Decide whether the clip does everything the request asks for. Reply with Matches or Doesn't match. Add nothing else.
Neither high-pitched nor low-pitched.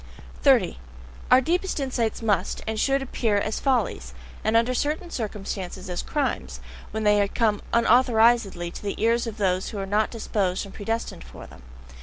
Doesn't match